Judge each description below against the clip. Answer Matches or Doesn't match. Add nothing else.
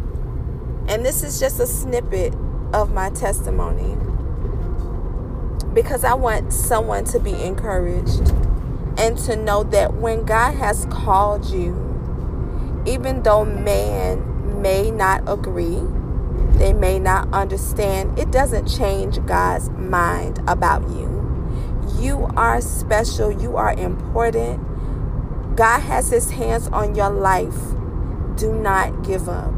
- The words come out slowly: Matches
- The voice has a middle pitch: Doesn't match